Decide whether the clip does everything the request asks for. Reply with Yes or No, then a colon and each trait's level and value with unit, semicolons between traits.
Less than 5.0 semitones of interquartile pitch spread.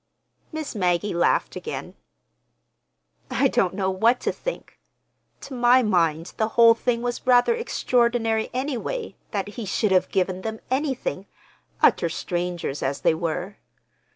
No: average, 5.3 semitones